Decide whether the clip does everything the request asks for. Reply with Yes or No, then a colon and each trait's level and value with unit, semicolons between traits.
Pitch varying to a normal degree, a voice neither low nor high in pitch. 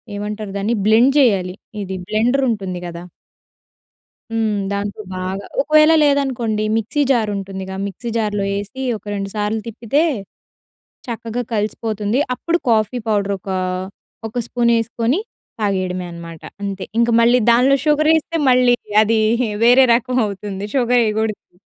No: average, 3.5 semitones; high, 220 Hz